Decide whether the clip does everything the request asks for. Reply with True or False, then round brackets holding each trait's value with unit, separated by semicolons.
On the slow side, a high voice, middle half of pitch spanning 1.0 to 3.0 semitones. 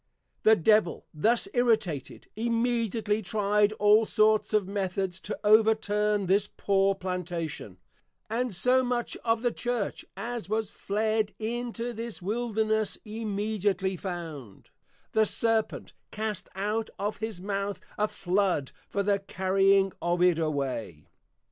True (125 wpm; 210 Hz; 2.7 semitones)